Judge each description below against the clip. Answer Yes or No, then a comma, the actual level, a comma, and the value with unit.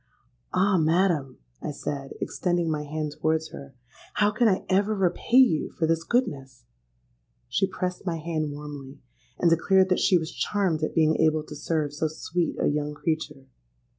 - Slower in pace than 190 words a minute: Yes, average, 165 wpm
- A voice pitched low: No, medium, 160 Hz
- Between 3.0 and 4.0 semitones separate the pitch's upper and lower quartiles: Yes, average, 3.7 semitones